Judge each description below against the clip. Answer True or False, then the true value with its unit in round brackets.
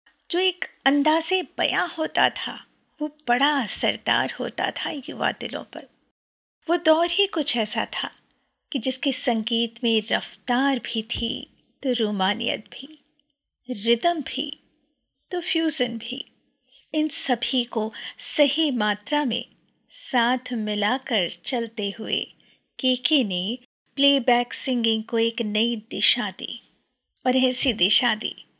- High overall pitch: True (250 Hz)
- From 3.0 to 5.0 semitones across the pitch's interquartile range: True (4.1 semitones)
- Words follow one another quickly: False (120 wpm)